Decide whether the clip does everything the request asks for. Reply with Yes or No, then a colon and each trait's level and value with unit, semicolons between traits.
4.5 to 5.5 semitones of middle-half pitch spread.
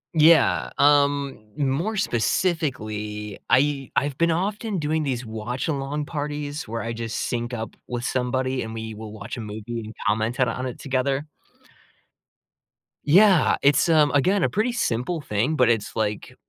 Yes: average, 4.9 semitones